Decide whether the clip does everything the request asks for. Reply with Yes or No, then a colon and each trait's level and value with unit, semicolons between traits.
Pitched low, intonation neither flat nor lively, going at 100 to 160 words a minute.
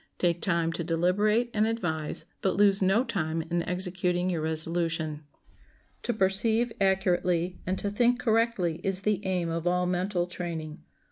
No: medium, 180 Hz; average, 3.2 semitones; average, 150 wpm